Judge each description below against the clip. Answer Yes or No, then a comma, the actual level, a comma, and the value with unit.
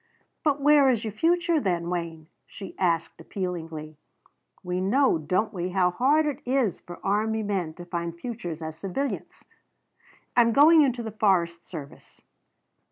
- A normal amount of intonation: No, wide, 6.8 semitones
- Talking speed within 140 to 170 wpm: Yes, average, 150 wpm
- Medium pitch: No, high, 195 Hz